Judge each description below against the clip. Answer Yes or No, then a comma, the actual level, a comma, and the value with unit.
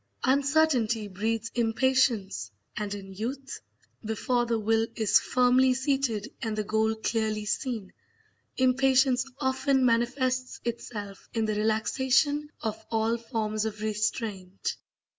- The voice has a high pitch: Yes, high, 230 Hz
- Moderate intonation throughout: Yes, average, 3.2 semitones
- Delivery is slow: Yes, slow, 115 wpm